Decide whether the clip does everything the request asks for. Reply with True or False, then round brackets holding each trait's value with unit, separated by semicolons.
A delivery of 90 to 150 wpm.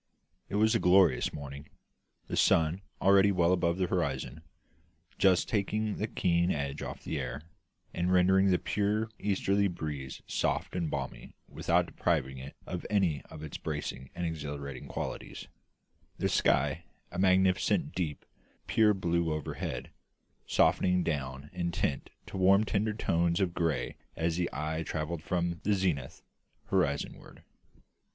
True (145 wpm)